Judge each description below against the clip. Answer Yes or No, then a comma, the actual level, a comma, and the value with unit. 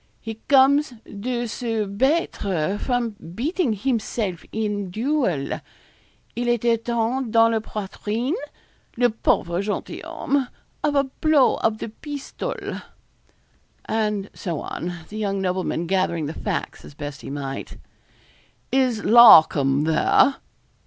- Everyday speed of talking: No, slow, 125 wpm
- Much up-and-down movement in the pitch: No, average, 4.8 semitones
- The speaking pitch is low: No, high, 220 Hz